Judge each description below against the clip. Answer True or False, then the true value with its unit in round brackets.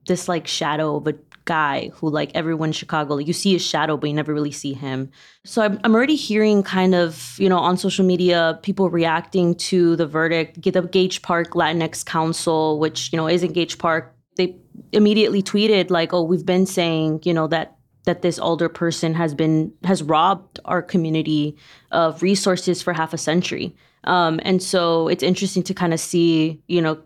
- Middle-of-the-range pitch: True (170 Hz)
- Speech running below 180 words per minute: False (195 wpm)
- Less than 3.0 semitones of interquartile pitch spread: True (2.5 semitones)